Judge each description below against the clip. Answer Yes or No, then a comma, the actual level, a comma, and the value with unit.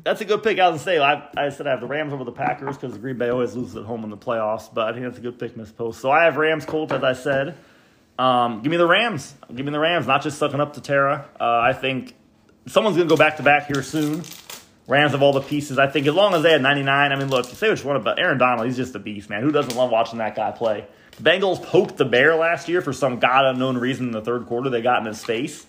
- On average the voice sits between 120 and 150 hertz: Yes, low, 135 Hz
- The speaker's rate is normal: No, fast, 305 wpm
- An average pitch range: Yes, average, 3.8 semitones